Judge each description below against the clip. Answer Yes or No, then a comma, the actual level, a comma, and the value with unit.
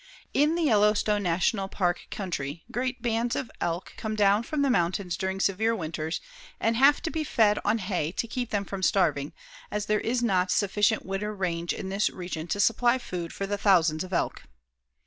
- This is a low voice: No, high, 200 Hz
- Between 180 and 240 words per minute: Yes, average, 190 wpm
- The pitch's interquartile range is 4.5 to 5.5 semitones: No, average, 4.1 semitones